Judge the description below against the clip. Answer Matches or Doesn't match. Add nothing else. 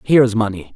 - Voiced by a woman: Doesn't match